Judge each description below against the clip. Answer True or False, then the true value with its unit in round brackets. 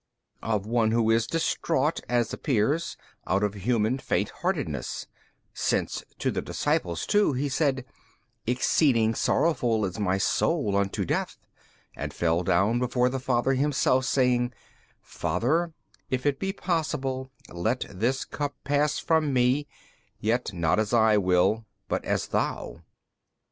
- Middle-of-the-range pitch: False (125 Hz)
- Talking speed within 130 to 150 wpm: True (140 wpm)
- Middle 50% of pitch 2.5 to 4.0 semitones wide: False (4.6 semitones)